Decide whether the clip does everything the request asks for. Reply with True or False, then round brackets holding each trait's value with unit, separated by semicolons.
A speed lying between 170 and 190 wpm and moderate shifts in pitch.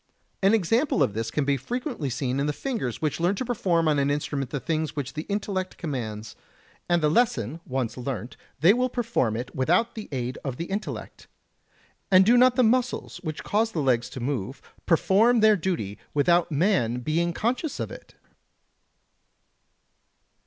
False (175 wpm; 8.0 semitones)